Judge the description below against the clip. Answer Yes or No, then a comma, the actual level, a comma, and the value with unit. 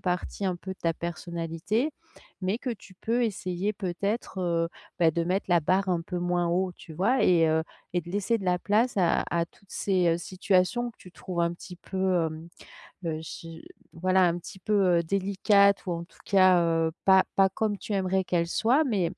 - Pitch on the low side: No, medium, 185 Hz